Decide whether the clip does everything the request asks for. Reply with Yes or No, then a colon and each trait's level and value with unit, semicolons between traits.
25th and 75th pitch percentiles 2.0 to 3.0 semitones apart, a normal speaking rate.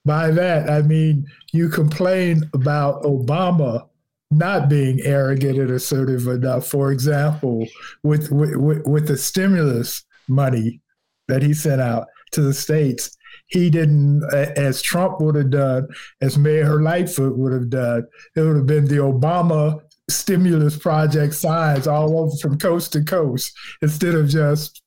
Yes: narrow, 2.4 semitones; average, 145 wpm